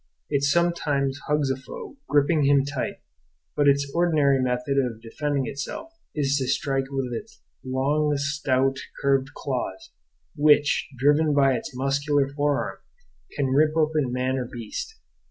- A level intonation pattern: Yes, narrow, 1.8 semitones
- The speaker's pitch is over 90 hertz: Yes, medium, 140 Hz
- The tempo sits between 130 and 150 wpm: Yes, average, 140 wpm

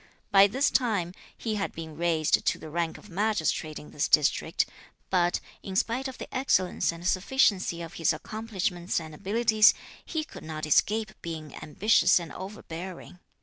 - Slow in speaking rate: No, average, 160 wpm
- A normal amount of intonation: Yes, average, 4.7 semitones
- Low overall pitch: No, medium, 185 Hz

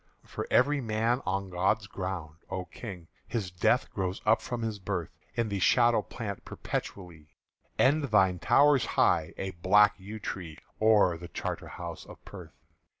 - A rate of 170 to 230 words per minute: No, average, 150 wpm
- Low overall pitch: Yes, low, 100 Hz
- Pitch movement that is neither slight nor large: Yes, average, 3.8 semitones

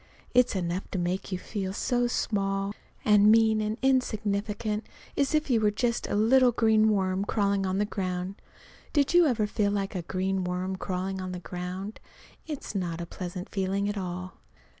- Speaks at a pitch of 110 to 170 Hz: No, high, 200 Hz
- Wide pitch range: No, average, 2.8 semitones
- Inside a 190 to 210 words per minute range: No, average, 180 wpm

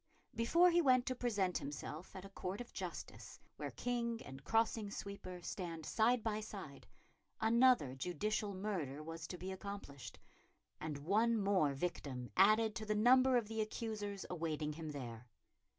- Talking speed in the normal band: Yes, average, 155 wpm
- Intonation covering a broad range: Yes, wide, 6.1 semitones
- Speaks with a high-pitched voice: Yes, high, 200 Hz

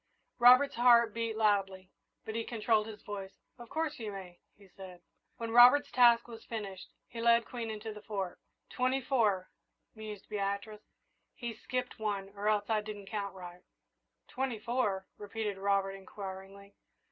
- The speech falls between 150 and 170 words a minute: Yes, average, 155 wpm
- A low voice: No, high, 215 Hz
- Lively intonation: No, average, 3.0 semitones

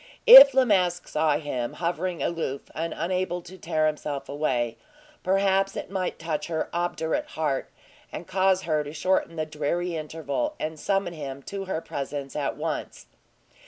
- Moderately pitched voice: Yes, medium, 165 Hz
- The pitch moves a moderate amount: Yes, average, 3.7 semitones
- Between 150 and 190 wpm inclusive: Yes, average, 160 wpm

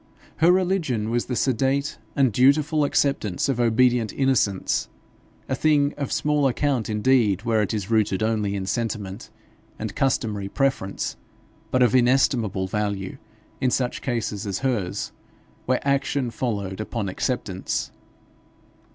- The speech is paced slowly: Yes, slow, 130 wpm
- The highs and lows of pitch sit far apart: No, average, 4.5 semitones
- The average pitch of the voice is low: Yes, low, 120 Hz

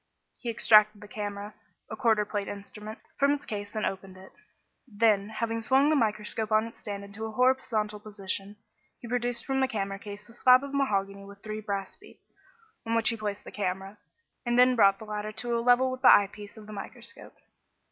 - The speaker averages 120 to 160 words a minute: No, fast, 205 wpm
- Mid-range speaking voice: No, high, 215 Hz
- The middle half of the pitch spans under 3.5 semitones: Yes, average, 2.7 semitones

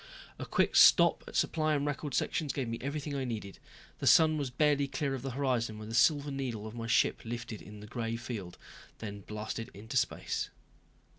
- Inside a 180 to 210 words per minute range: Yes, average, 200 wpm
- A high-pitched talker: No, low, 125 Hz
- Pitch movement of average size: Yes, average, 4.2 semitones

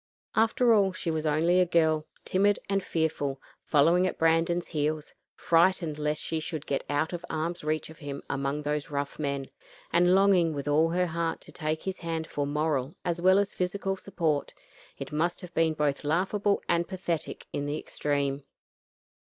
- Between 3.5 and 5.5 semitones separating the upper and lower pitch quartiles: No, average, 3.1 semitones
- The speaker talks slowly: No, average, 180 wpm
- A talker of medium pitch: Yes, medium, 160 Hz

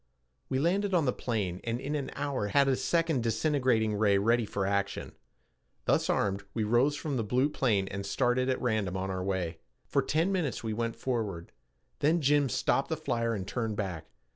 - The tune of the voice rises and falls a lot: Yes, wide, 5.7 semitones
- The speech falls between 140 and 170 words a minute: No, average, 190 wpm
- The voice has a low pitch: Yes, low, 115 Hz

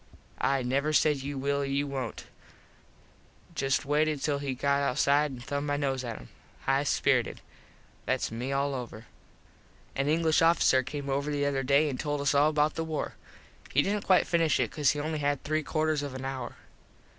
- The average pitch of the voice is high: No, medium, 140 Hz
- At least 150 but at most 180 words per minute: No, average, 190 wpm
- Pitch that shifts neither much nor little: No, narrow, 1.8 semitones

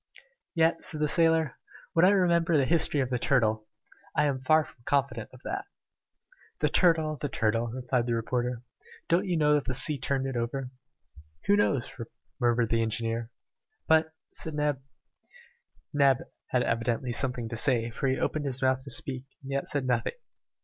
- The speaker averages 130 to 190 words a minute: Yes, average, 175 wpm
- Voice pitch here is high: No, low, 135 Hz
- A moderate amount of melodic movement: Yes, average, 4.1 semitones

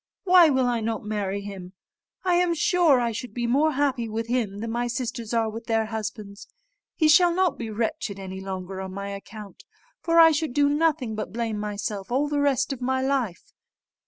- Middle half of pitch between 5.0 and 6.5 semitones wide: Yes, wide, 5.5 semitones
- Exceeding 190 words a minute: Yes, average, 200 wpm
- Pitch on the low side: No, high, 235 Hz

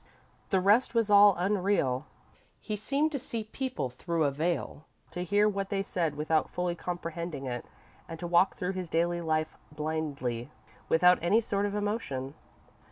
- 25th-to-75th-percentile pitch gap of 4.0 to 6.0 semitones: Yes, average, 4.5 semitones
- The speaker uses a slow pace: No, average, 165 wpm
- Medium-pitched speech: Yes, medium, 175 Hz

